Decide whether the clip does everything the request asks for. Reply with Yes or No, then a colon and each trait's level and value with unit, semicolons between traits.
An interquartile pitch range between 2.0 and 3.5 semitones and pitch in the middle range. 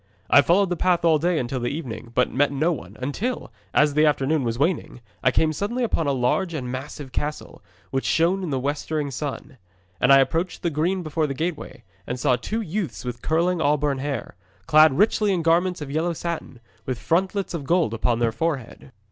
No: average, 4.4 semitones; medium, 150 Hz